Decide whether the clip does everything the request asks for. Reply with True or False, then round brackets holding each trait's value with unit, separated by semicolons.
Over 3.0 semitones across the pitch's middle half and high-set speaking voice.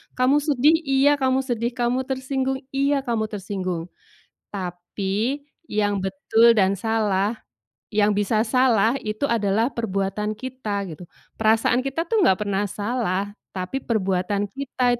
True (4.6 semitones; 225 Hz)